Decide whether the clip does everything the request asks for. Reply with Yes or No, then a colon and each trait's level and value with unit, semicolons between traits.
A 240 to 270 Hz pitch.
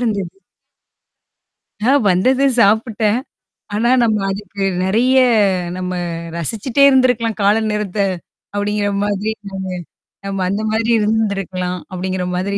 No: high, 210 Hz